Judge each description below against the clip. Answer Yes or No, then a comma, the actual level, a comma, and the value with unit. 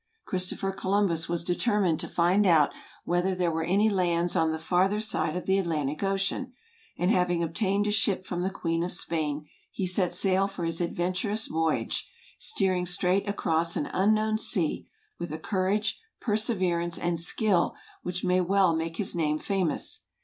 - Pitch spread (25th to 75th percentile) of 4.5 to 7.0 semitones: No, average, 2.7 semitones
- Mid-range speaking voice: Yes, medium, 180 Hz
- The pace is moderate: Yes, average, 165 wpm